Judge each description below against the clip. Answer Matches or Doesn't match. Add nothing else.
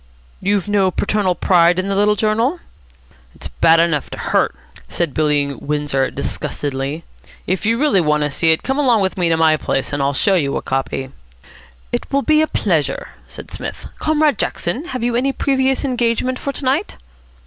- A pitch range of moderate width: Doesn't match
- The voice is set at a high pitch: Matches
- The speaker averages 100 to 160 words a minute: Doesn't match